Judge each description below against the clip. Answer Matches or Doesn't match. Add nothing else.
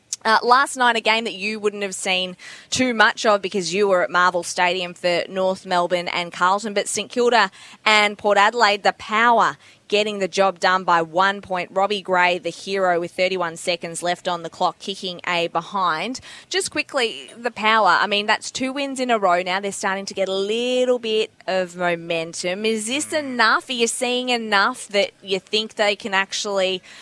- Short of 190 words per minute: Doesn't match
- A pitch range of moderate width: Matches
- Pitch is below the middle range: Doesn't match